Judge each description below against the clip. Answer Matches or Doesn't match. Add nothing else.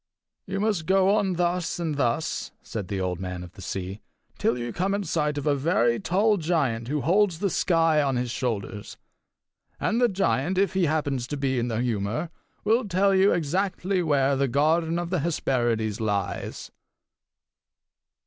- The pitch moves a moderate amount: Doesn't match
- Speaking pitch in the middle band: Matches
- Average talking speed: Matches